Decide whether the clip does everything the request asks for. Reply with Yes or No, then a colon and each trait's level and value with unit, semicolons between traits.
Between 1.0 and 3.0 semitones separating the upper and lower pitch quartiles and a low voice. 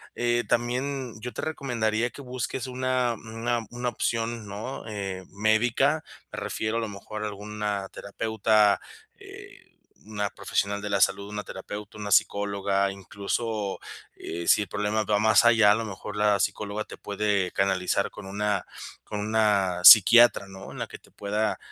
Yes: narrow, 2.4 semitones; low, 105 Hz